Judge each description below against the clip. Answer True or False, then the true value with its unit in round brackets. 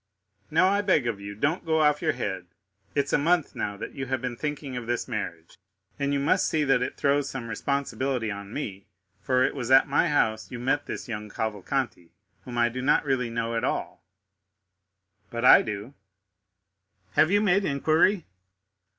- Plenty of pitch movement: False (4.3 semitones)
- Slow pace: False (185 wpm)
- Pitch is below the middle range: True (130 Hz)